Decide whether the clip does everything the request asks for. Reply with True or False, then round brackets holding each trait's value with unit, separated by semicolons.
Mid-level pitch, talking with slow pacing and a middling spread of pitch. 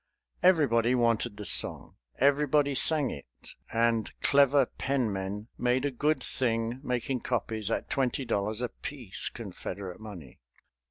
False (120 Hz; 120 wpm; 4.1 semitones)